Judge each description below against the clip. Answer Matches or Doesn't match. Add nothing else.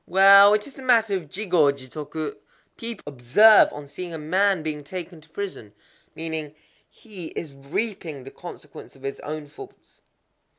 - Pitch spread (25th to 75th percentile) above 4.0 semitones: Matches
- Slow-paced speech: Doesn't match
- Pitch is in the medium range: Matches